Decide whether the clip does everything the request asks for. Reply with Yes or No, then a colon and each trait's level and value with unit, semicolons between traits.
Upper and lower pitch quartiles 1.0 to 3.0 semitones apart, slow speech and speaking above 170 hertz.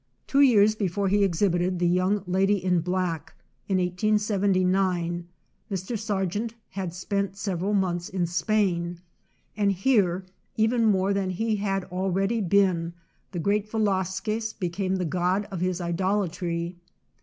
Yes: narrow, 2.4 semitones; slow, 130 wpm; high, 190 Hz